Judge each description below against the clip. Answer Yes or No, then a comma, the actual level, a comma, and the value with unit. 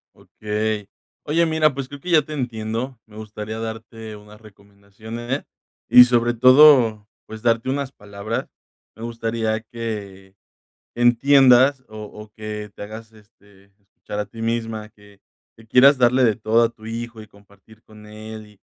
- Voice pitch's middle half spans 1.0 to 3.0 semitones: Yes, narrow, 2.4 semitones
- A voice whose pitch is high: No, low, 110 Hz